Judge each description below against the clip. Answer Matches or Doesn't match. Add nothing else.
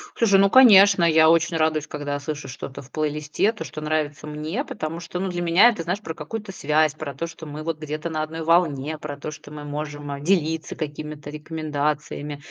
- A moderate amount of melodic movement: Doesn't match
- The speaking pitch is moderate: Matches